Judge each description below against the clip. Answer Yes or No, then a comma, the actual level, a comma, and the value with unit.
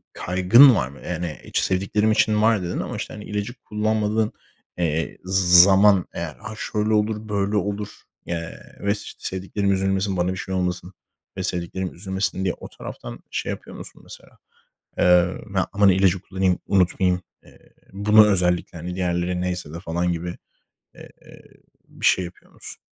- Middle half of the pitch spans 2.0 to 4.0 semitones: Yes, narrow, 2.6 semitones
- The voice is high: No, very low, 95 Hz